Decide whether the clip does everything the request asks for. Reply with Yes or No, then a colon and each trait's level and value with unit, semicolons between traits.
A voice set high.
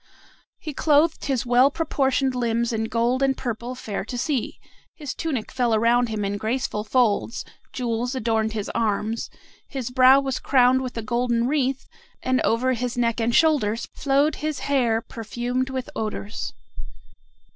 Yes: high, 245 Hz